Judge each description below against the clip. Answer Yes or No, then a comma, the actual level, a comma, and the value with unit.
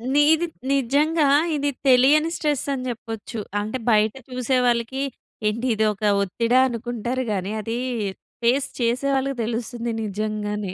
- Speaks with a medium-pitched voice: No, high, 240 Hz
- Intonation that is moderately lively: Yes, average, 3.6 semitones